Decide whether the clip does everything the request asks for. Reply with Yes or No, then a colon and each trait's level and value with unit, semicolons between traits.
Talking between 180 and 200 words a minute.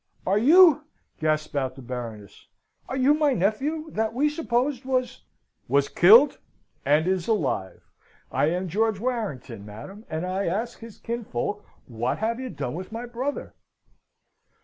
No: average, 150 wpm